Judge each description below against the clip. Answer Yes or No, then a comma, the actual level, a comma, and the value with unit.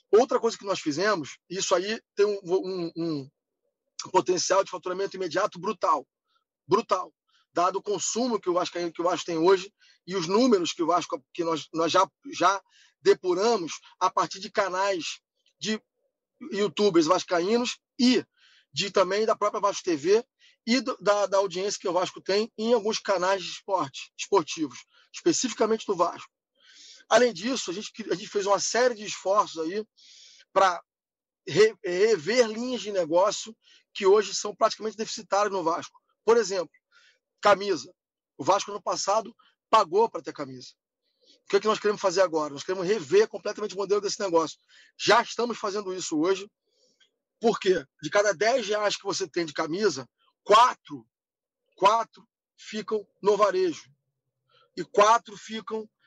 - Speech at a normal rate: Yes, average, 155 wpm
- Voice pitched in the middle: No, high, 210 Hz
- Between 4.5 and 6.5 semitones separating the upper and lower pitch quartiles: Yes, average, 4.8 semitones